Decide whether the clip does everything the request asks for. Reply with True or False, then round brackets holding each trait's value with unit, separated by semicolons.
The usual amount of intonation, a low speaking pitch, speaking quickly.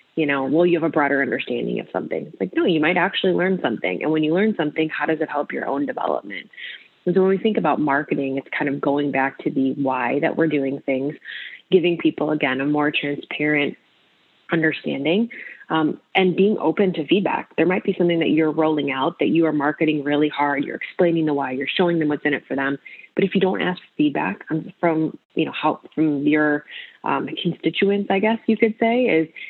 False (3.8 semitones; 160 Hz; 220 wpm)